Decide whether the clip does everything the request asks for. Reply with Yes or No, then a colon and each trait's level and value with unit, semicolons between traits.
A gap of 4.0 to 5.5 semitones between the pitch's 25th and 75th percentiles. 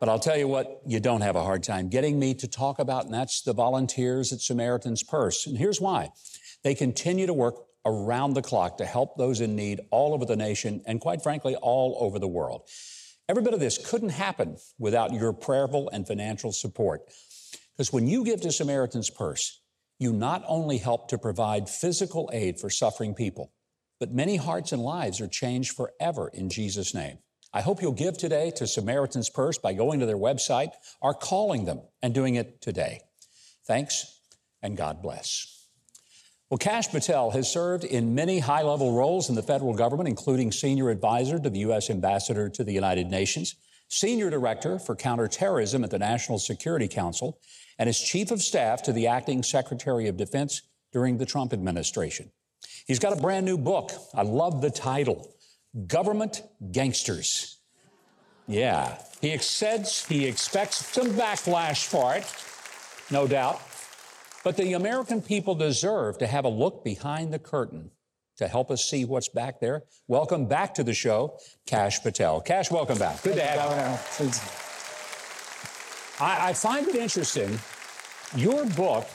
Yes: average, 5.2 semitones